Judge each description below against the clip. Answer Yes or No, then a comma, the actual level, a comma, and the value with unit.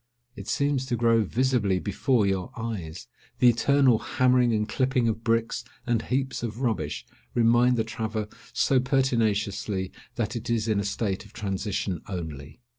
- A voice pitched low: Yes, low, 115 Hz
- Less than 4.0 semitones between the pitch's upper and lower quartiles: Yes, average, 3.6 semitones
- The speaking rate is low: No, average, 155 wpm